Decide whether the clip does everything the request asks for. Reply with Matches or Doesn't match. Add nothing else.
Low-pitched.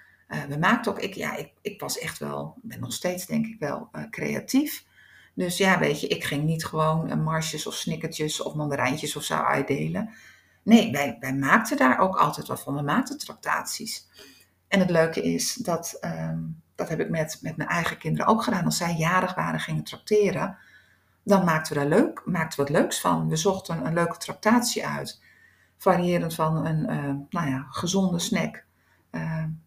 Doesn't match